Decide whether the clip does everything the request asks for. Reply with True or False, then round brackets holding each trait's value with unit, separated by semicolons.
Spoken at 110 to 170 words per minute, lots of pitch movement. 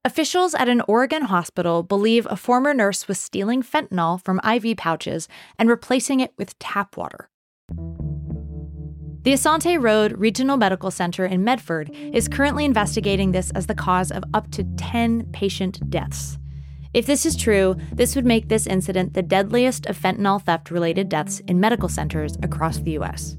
True (165 wpm; 6.2 semitones)